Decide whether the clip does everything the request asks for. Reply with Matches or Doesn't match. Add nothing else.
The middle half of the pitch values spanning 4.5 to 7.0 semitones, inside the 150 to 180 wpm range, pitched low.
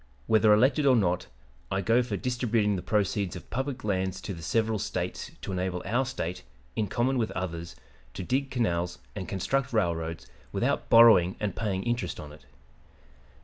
Matches